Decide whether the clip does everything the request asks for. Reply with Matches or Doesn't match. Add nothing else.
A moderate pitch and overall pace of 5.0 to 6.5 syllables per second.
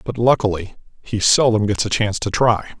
Doesn't match